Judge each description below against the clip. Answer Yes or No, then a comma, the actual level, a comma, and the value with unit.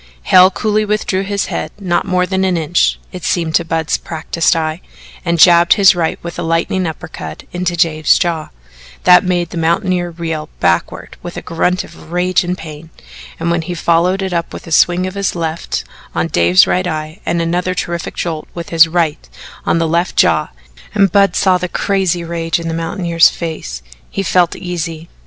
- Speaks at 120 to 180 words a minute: No, average, 190 wpm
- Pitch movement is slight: Yes, narrow, 1.9 semitones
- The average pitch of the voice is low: No, medium, 170 Hz